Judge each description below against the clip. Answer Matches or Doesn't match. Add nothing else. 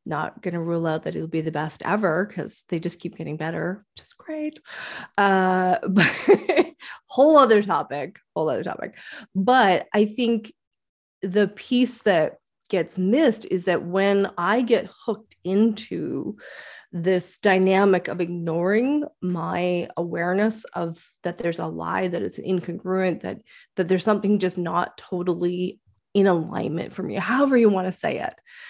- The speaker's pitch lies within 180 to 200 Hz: Matches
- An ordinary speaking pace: Matches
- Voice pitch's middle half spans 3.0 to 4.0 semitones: Matches